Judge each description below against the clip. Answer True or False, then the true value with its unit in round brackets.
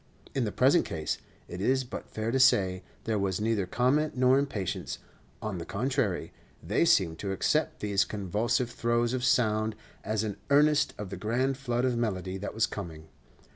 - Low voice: True (110 Hz)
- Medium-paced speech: True (175 wpm)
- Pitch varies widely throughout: False (4.6 semitones)